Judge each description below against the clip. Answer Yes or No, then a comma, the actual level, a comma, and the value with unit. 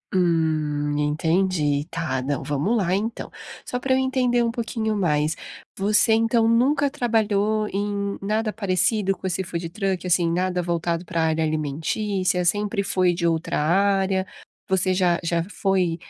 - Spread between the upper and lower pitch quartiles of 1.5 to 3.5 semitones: No, average, 4.2 semitones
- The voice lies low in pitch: No, medium, 185 Hz